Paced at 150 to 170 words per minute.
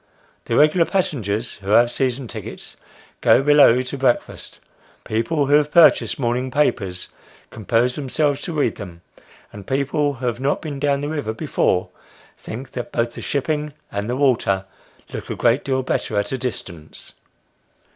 Yes: average, 160 wpm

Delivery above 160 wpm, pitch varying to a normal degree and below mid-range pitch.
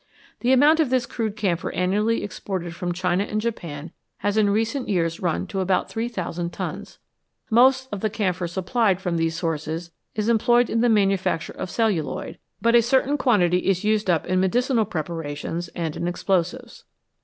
No: average, 170 wpm; average, 4.7 semitones; high, 195 Hz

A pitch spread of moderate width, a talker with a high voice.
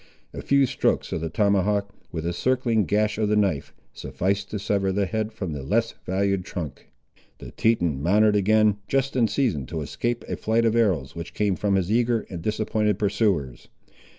No: average, 3.3 semitones; low, 105 Hz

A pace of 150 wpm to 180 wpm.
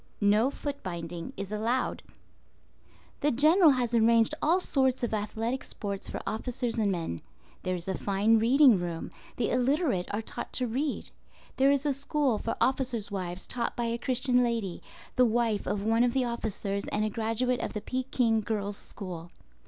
Yes: average, 175 wpm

